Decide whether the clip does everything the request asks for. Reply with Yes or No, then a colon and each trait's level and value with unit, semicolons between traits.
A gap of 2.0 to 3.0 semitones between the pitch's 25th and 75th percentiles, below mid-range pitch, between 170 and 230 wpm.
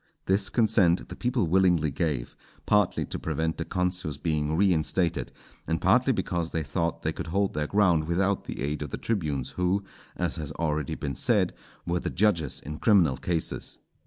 No: average, 3.8 semitones; very low, 85 Hz; average, 175 wpm